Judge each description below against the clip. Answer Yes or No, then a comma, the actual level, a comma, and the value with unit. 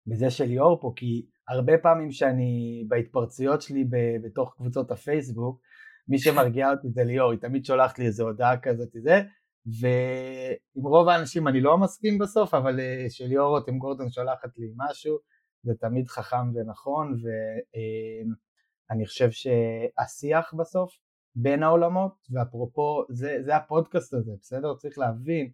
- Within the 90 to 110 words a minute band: No, average, 145 wpm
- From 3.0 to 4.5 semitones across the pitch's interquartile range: Yes, average, 4.0 semitones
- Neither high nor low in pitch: No, low, 130 Hz